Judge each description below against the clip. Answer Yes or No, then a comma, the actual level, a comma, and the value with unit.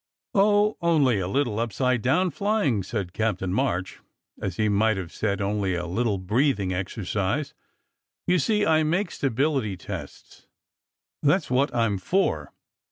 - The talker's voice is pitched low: Yes, low, 115 Hz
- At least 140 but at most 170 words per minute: Yes, average, 150 wpm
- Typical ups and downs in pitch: No, wide, 7.5 semitones